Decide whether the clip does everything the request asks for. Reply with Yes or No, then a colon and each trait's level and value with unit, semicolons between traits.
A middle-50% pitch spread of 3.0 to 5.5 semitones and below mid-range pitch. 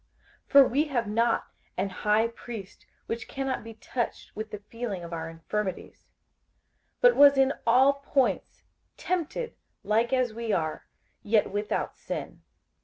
No: average, 4.4 semitones; high, 230 Hz